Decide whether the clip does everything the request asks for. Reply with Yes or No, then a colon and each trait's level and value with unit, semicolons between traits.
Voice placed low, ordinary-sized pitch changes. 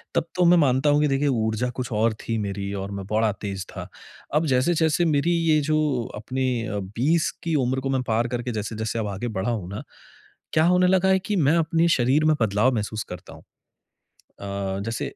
No: low, 125 Hz; wide, 6.2 semitones